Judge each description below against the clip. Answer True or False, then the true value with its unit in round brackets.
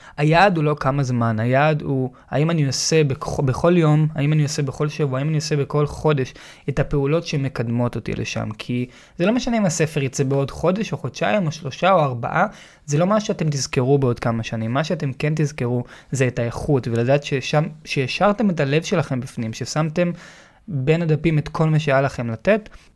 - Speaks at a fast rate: True (190 wpm)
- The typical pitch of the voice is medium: True (145 Hz)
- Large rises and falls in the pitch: False (3.3 semitones)